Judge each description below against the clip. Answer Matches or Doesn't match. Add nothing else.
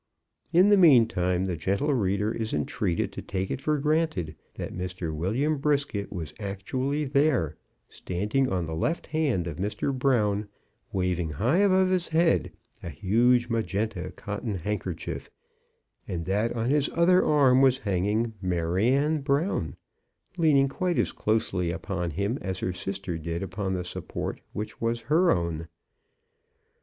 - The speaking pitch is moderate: Doesn't match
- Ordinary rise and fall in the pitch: Doesn't match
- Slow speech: Doesn't match